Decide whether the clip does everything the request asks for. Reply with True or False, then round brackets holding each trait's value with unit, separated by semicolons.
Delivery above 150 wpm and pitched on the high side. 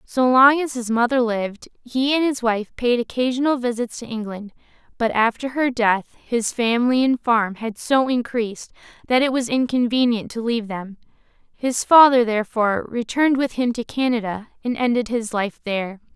True (170 wpm; 240 Hz)